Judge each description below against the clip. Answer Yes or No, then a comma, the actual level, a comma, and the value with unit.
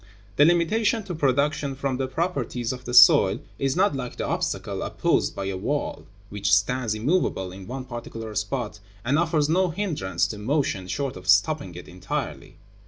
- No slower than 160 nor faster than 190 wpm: Yes, average, 170 wpm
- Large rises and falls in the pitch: Yes, wide, 6.4 semitones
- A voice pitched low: Yes, low, 130 Hz